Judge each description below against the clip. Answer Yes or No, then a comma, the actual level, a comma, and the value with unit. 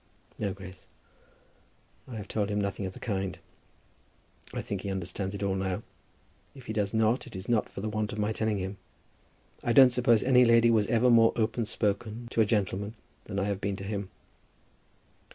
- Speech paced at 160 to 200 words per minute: Yes, average, 195 wpm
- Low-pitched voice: Yes, low, 105 Hz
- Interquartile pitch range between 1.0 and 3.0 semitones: Yes, narrow, 2.6 semitones